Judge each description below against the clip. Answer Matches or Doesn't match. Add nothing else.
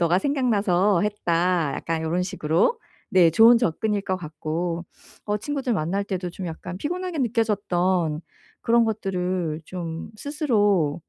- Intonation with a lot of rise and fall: Doesn't match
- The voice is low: Doesn't match